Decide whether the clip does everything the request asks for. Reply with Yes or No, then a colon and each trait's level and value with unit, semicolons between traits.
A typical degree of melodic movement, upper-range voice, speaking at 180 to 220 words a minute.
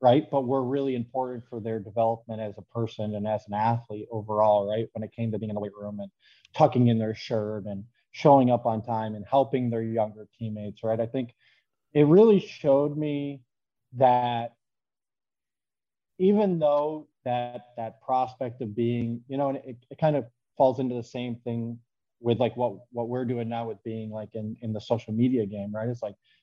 No: average, 3.0 semitones; low, 120 Hz; average, 200 wpm